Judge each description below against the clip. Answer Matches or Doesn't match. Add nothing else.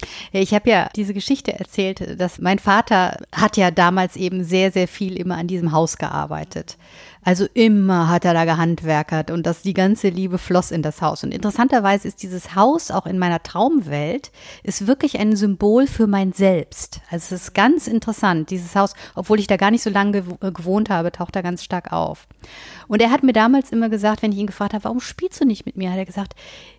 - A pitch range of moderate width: Matches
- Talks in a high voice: Matches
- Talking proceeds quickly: Matches